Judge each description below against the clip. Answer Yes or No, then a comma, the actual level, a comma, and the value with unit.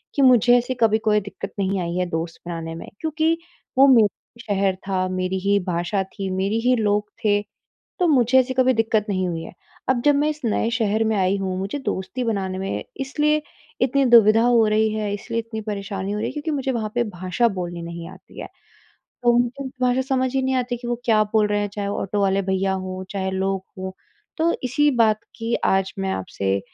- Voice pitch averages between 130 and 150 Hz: No, high, 210 Hz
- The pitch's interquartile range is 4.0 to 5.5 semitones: Yes, average, 4.4 semitones